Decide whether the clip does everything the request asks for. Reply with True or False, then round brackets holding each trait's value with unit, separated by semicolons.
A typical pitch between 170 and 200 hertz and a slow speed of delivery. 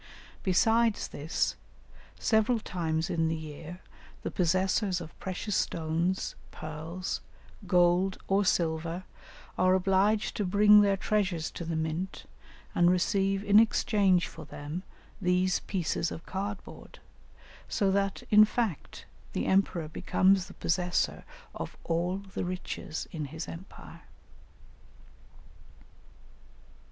True (185 Hz; 115 wpm)